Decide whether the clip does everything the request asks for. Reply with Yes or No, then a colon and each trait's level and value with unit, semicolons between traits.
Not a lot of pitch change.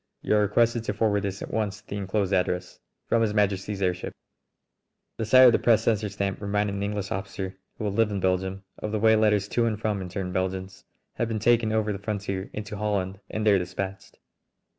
Yes: narrow, 2.0 semitones